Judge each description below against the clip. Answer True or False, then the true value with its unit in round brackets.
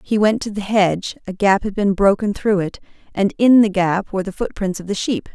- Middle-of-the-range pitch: False (200 Hz)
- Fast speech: True (245 wpm)